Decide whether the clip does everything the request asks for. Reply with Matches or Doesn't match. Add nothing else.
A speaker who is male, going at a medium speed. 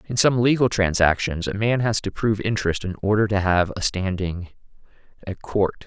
Matches